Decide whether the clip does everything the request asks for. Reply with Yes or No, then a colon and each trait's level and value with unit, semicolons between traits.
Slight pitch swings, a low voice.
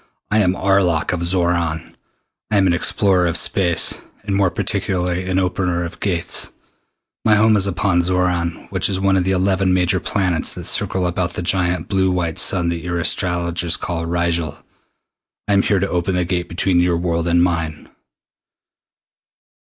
Yes: narrow, 1.8 semitones; very low, 90 Hz